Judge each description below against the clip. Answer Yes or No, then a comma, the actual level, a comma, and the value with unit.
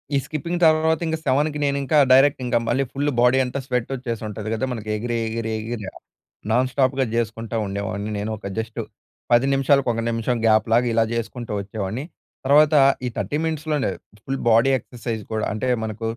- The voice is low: Yes, low, 120 Hz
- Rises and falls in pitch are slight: No, average, 3.5 semitones